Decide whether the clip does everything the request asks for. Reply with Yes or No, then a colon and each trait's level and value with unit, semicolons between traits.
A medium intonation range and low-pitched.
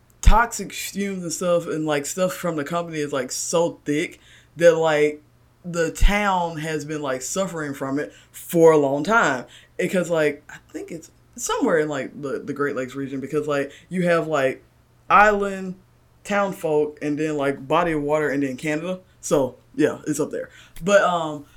No: average, 3.4 semitones; medium, 155 Hz